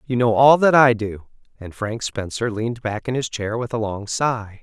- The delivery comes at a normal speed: No, fast, 235 wpm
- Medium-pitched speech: No, low, 115 Hz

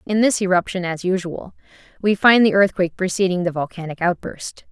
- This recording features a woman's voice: Yes, female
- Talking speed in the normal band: Yes, average, 165 wpm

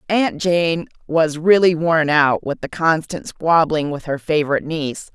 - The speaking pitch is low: No, medium, 160 Hz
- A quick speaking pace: No, average, 165 wpm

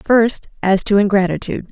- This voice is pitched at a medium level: No, high, 200 Hz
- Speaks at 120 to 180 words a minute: Yes, average, 140 wpm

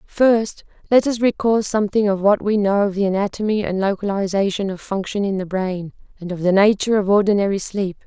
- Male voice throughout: No, female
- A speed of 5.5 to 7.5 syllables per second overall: Yes, 5.7 syllables/s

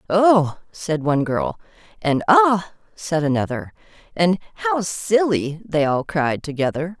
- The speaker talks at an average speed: No, slow, 130 wpm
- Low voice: No, medium, 170 Hz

